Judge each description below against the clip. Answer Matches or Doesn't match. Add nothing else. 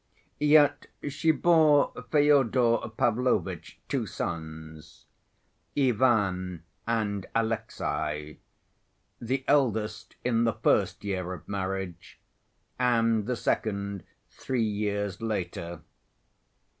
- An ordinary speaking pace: Doesn't match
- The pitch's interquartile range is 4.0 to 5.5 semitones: Matches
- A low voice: Matches